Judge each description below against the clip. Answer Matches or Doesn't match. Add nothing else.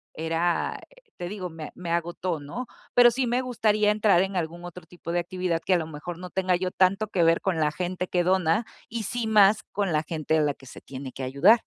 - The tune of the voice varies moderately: Matches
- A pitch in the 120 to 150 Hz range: Doesn't match